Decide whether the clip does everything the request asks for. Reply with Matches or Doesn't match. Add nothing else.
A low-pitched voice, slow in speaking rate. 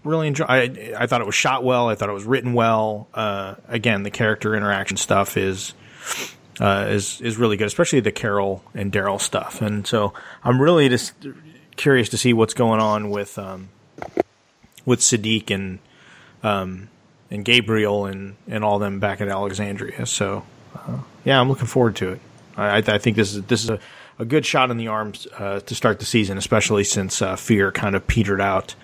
Doesn't match